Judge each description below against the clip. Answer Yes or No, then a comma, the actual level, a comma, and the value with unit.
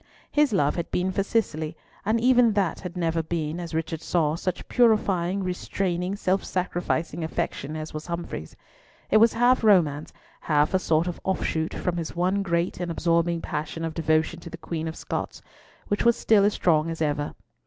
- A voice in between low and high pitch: Yes, medium, 170 Hz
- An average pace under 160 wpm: No, average, 185 wpm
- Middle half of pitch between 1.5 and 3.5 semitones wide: Yes, average, 3.2 semitones